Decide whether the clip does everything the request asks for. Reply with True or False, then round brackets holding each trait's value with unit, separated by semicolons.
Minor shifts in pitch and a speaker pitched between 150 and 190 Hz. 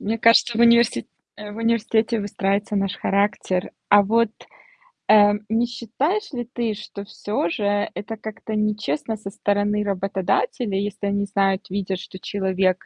False (2.3 semitones; 205 Hz)